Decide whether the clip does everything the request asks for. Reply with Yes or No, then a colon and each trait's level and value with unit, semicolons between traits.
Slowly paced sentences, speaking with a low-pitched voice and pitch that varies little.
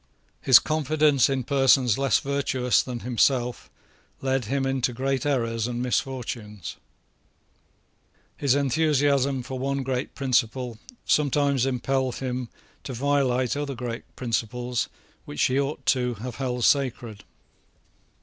Yes: slow, 120 wpm; low, 130 Hz; narrow, 2.1 semitones